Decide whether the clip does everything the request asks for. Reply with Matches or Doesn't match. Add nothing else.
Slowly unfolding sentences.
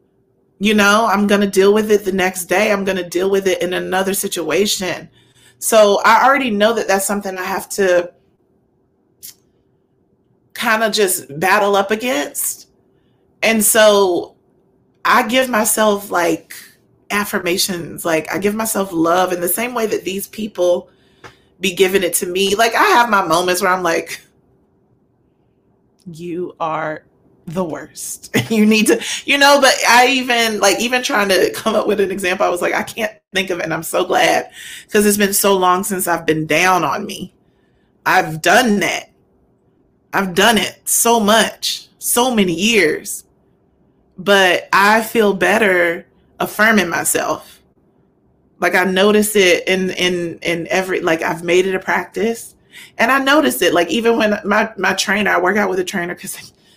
Doesn't match